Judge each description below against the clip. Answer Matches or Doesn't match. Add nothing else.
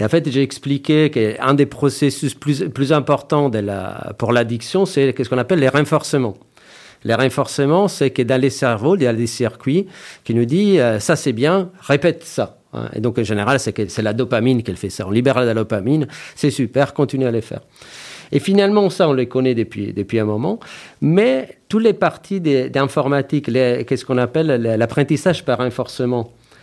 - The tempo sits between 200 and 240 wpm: Doesn't match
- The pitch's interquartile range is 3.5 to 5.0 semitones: Matches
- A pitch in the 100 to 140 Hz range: Matches